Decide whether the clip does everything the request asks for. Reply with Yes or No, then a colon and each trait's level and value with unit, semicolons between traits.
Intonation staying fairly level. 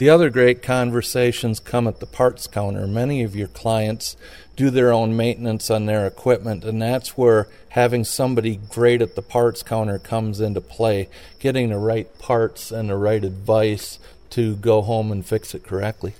Yes: narrow, 2.3 semitones